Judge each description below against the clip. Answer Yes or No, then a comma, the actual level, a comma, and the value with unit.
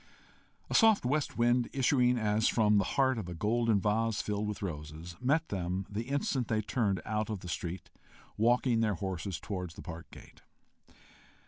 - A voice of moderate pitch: No, low, 105 Hz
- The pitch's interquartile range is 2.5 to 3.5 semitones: No, average, 4.2 semitones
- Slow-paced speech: No, average, 175 wpm